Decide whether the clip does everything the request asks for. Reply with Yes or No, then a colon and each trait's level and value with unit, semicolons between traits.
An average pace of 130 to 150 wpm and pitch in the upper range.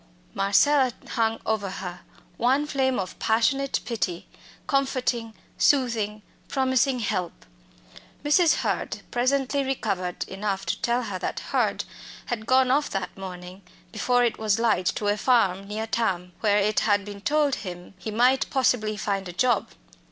Yes: average, 145 wpm; high, 220 Hz